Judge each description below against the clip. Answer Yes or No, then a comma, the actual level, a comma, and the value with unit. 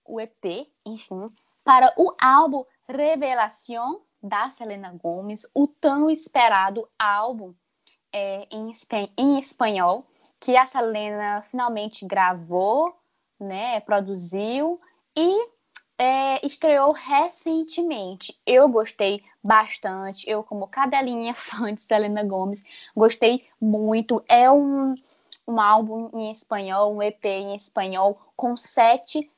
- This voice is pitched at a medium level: No, high, 225 Hz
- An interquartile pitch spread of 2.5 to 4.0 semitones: No, average, 5.0 semitones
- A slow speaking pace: Yes, slow, 110 wpm